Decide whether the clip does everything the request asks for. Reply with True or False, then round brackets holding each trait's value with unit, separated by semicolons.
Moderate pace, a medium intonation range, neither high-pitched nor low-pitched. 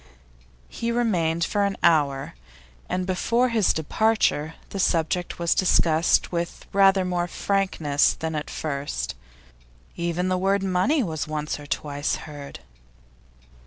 False (125 wpm; 3.9 semitones; 175 Hz)